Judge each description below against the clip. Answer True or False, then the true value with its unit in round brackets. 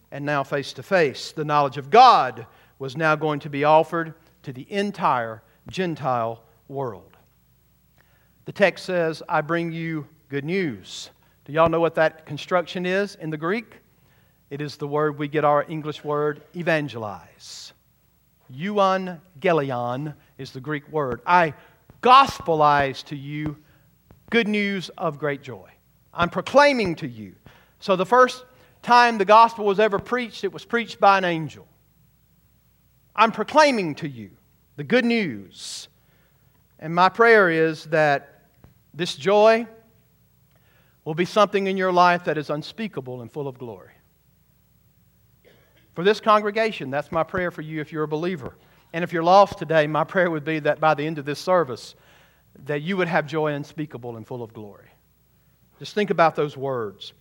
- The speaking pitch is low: False (155 Hz)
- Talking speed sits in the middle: True (160 wpm)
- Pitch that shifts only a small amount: False (4.4 semitones)